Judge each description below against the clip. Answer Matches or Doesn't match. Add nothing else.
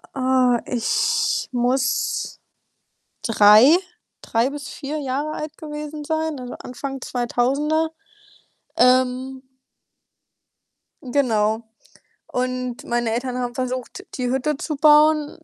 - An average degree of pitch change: Matches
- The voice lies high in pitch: Matches